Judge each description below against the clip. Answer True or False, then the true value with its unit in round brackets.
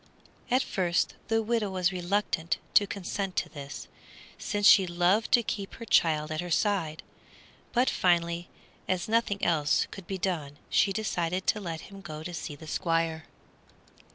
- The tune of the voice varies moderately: True (3.6 semitones)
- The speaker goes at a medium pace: True (160 wpm)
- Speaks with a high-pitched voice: False (180 Hz)